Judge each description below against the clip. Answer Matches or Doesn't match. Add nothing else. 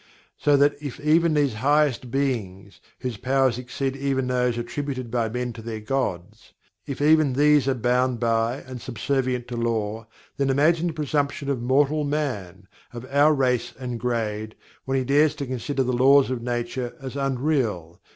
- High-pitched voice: Doesn't match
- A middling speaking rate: Matches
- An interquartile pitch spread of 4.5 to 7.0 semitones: Doesn't match